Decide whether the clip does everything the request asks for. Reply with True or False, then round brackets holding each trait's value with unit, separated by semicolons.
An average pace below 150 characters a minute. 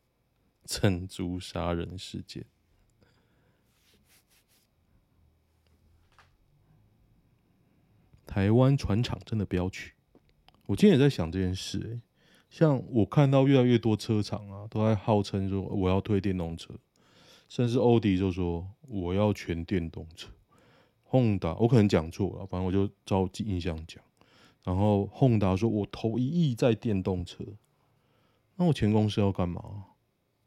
False (190 characters per minute)